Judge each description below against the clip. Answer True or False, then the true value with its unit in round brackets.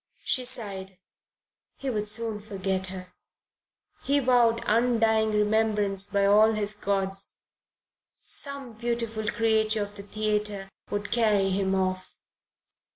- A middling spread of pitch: False (2.3 semitones)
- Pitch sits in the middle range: False (210 Hz)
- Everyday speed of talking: False (115 wpm)